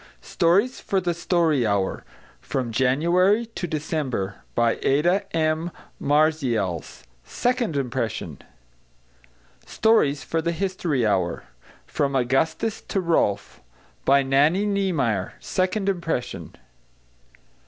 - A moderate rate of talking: No, slow, 100 wpm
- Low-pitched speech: No, medium, 155 Hz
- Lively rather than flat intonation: Yes, wide, 6.4 semitones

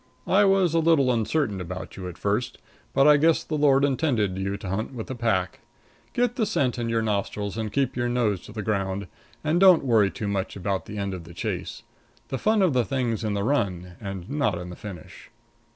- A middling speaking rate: No, fast, 220 wpm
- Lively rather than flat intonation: Yes, wide, 6.3 semitones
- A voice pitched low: Yes, low, 110 Hz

